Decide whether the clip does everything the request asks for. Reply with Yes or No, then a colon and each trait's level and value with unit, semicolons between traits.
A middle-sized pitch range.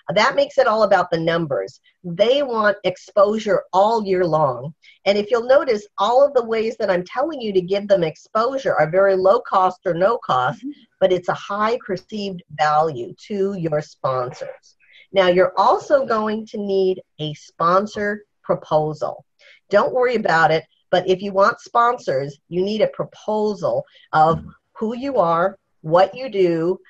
Yes: average, 3.7 semitones